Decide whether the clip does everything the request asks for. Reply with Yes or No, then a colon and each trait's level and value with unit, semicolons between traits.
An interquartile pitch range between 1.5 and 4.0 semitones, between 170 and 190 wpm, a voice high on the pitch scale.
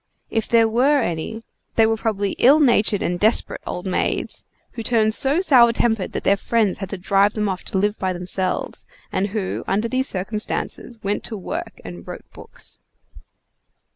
Yes: average, 3.2 semitones; average, 175 wpm; high, 215 Hz